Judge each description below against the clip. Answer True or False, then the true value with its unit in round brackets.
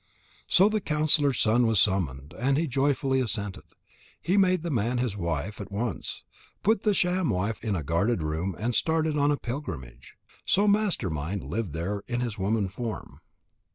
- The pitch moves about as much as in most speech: False (7.5 semitones)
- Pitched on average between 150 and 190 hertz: False (120 Hz)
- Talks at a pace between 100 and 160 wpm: False (175 wpm)